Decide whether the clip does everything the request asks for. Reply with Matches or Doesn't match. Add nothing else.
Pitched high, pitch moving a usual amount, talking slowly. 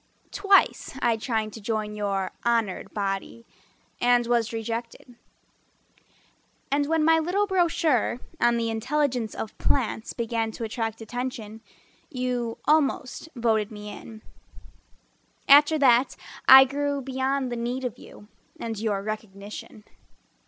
Matches